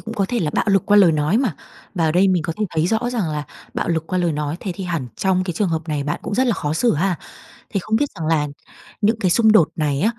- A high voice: No, medium, 180 Hz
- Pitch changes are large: No, average, 4.8 semitones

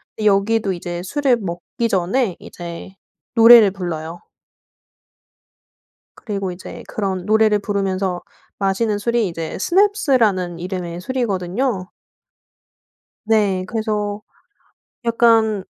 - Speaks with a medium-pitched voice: No, high, 200 Hz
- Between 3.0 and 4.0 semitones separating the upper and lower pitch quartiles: Yes, average, 3.6 semitones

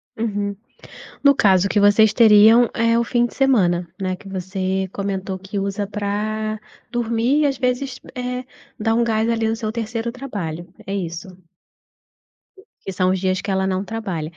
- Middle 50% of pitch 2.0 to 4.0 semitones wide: Yes, average, 3.4 semitones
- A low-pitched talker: No, high, 210 Hz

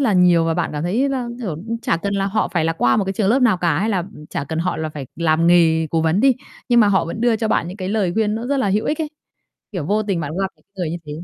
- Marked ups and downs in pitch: No, average, 4.8 semitones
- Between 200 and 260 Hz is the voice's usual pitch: No, high, 190 Hz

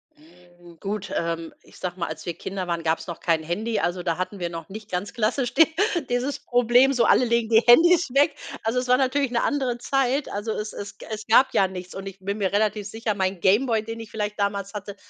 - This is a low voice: No, high, 210 Hz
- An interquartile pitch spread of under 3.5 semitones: No, average, 4.7 semitones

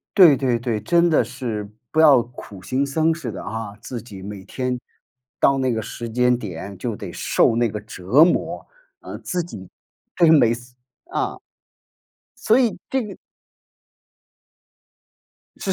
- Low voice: Yes, low, 125 Hz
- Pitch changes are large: Yes, wide, 6.6 semitones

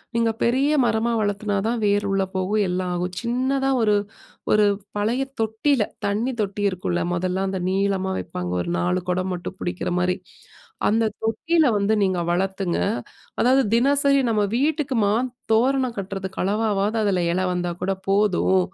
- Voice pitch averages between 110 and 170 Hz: No, high, 205 Hz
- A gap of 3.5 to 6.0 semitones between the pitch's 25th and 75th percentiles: Yes, average, 4.0 semitones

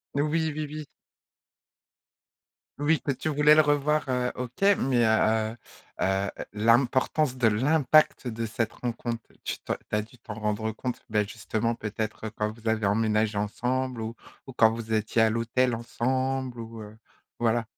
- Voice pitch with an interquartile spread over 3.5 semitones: No, average, 3.0 semitones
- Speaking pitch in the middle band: No, low, 115 Hz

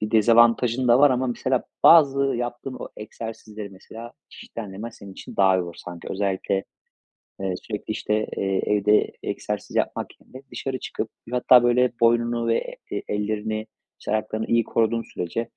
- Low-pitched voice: Yes, low, 115 Hz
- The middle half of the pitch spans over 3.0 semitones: No, narrow, 2.5 semitones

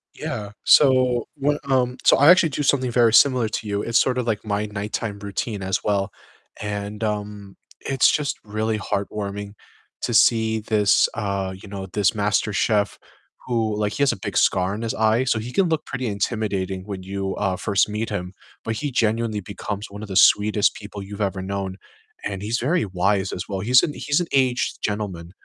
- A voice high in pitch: No, low, 105 Hz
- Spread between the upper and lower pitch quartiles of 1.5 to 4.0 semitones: Yes, average, 3.0 semitones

